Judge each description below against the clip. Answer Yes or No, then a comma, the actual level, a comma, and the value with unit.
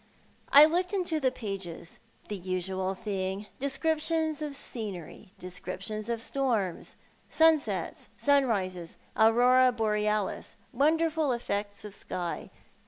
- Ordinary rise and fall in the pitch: No, wide, 6.7 semitones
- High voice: Yes, high, 225 Hz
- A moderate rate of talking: No, slow, 105 wpm